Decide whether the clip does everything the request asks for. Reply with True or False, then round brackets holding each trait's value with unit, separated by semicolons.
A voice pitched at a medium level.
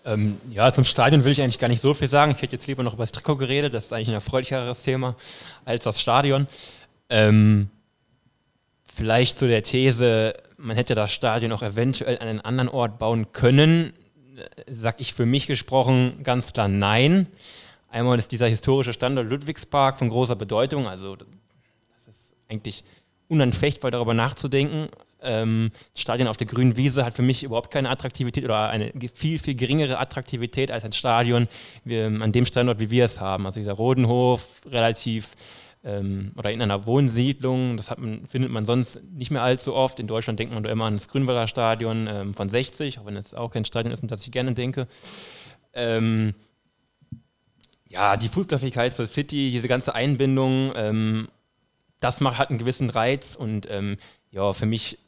False (120 Hz)